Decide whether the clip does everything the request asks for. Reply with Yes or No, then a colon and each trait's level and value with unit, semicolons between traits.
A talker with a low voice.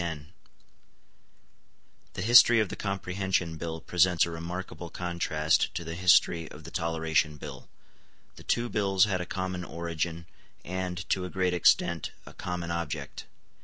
Yes: very low, 90 Hz